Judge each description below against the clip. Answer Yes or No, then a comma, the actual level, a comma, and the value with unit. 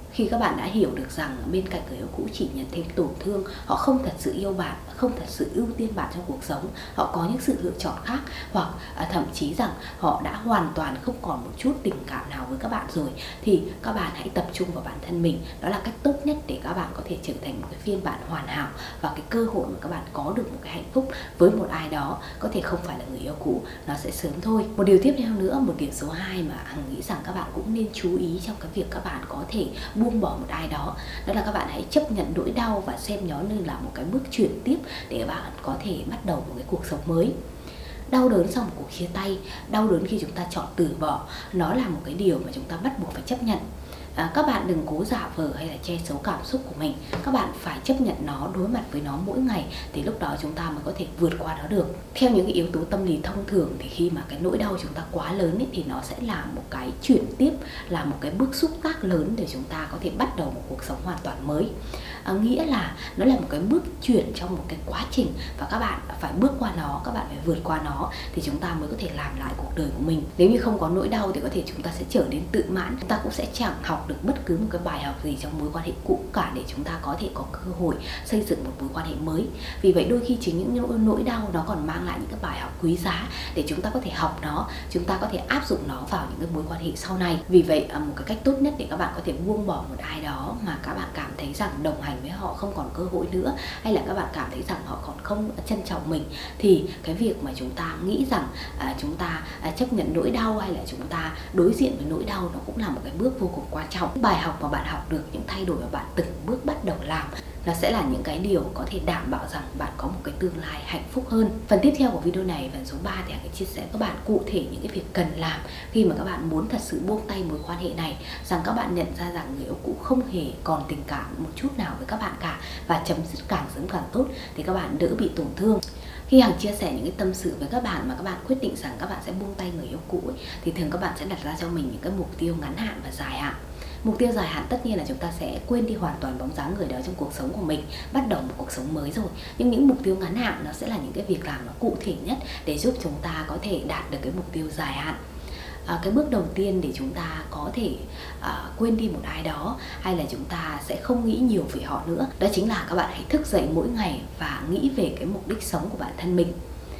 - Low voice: No, high, 190 Hz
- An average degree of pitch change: No, wide, 5.9 semitones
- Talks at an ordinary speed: No, fast, 290 wpm